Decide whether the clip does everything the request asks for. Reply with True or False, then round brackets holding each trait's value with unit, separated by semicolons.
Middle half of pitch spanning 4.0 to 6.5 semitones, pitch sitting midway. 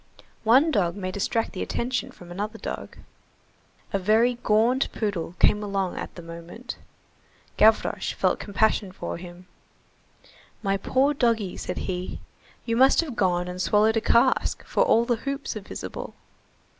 False (4.3 semitones; 215 Hz)